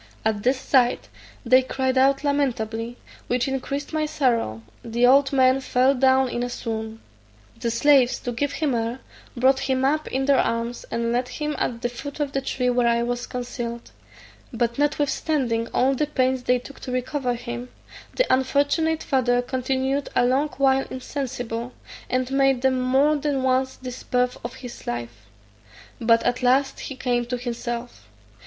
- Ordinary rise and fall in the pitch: No, narrow, 2.1 semitones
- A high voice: Yes, very high, 255 Hz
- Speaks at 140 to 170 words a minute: Yes, average, 165 wpm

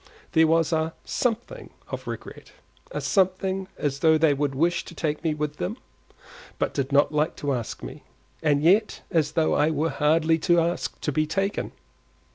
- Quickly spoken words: No, average, 180 wpm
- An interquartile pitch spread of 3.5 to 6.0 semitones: No, narrow, 2.6 semitones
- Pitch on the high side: No, medium, 160 Hz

